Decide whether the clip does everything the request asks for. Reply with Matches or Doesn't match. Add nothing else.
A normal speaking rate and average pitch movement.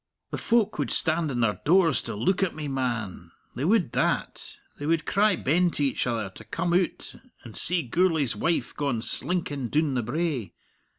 Doesn't match